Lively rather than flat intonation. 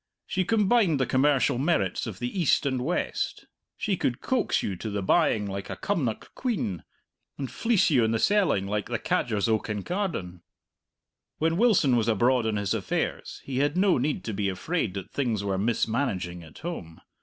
Yes: wide, 8.7 semitones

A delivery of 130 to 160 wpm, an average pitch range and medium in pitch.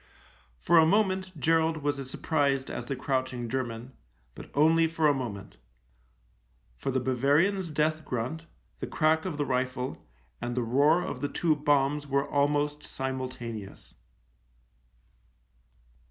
Yes: slow, 135 wpm; average, 3.6 semitones; medium, 145 Hz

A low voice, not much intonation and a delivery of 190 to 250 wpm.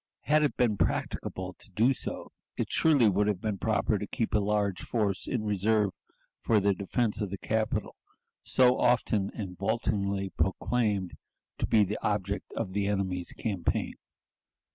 No: low, 105 Hz; narrow, 2.2 semitones; average, 160 wpm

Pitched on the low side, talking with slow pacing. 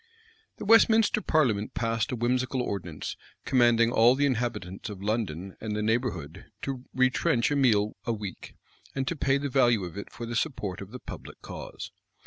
No: low, 115 Hz; average, 175 wpm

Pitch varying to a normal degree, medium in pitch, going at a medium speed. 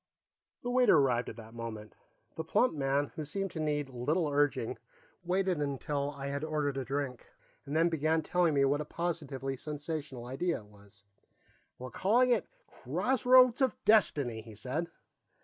Yes: average, 4.3 semitones; medium, 145 Hz; average, 165 wpm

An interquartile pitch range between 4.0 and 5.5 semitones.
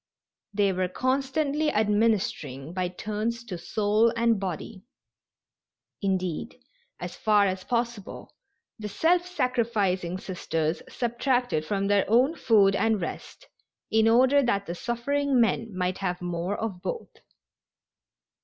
Yes: average, 4.4 semitones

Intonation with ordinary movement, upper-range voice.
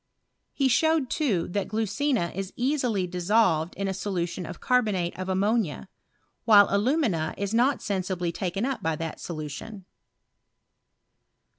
Yes: average, 4.8 semitones; high, 200 Hz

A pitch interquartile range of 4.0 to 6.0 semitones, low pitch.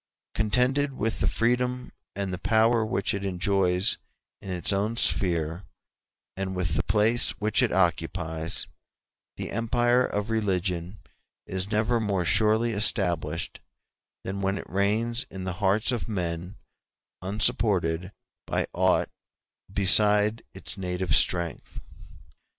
No: average, 3.4 semitones; low, 100 Hz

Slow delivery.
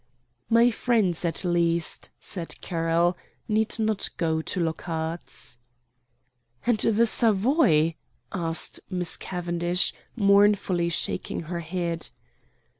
Yes: slow, 100 wpm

